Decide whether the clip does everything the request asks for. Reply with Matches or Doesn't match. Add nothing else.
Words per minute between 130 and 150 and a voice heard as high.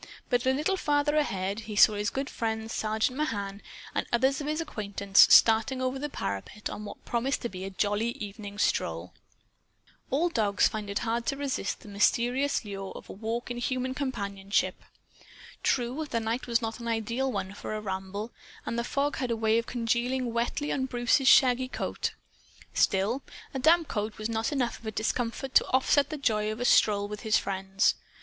Doesn't match